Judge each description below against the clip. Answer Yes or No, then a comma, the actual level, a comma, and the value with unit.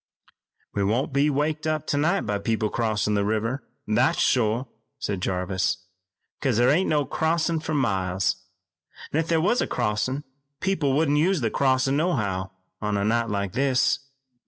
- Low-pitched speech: Yes, low, 130 Hz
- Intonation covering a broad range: Yes, wide, 6.2 semitones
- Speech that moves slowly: No, average, 160 wpm